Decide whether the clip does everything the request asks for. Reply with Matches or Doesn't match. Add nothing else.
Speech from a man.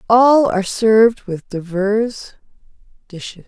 Doesn't match